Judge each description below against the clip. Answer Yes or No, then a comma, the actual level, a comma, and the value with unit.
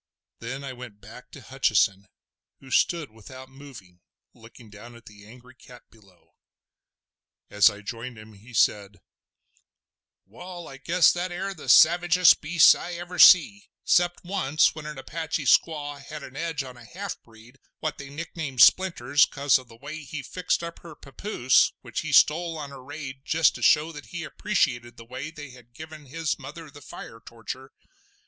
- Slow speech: No, average, 170 wpm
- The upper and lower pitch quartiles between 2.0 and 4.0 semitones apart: No, average, 5.1 semitones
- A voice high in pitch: No, medium, 140 Hz